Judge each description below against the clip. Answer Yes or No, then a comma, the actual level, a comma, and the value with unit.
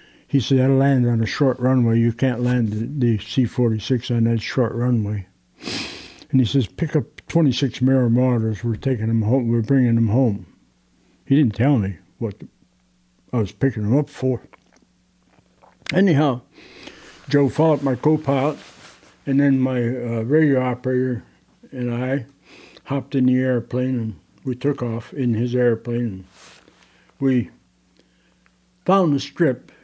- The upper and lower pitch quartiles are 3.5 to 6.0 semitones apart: No, average, 3.0 semitones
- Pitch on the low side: Yes, low, 125 Hz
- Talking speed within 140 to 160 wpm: Yes, average, 150 wpm